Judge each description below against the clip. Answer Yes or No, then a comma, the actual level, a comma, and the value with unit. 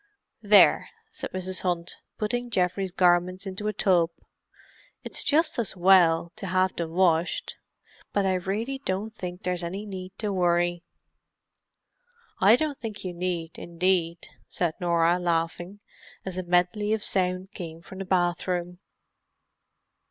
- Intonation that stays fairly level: Yes, narrow, 2.2 semitones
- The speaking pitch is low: No, medium, 185 Hz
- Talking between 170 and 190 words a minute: No, slow, 135 wpm